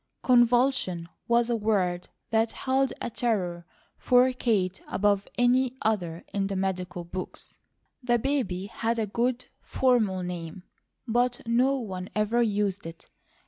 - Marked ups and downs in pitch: No, average, 4.6 semitones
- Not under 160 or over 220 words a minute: No, slow, 135 wpm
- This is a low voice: No, high, 220 Hz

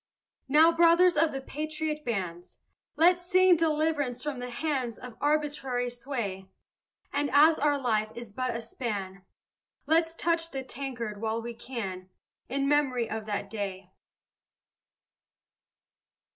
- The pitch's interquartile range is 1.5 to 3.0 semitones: No, average, 5.3 semitones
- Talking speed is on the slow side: Yes, slow, 130 wpm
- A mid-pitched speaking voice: No, very high, 265 Hz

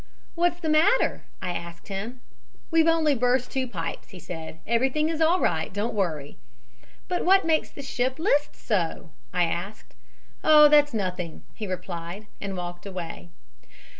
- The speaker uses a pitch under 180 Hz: No, high, 220 Hz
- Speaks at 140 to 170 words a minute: Yes, average, 160 wpm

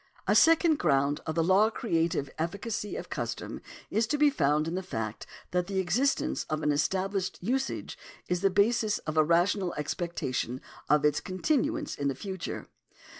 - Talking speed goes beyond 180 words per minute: No, average, 170 wpm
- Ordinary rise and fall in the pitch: No, wide, 5.7 semitones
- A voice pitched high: No, medium, 180 Hz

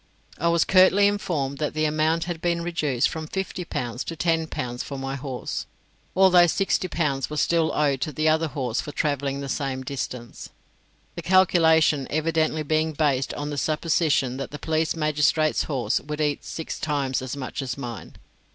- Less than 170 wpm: No, average, 180 wpm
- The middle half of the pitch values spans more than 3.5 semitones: No, average, 3.0 semitones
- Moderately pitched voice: Yes, medium, 150 Hz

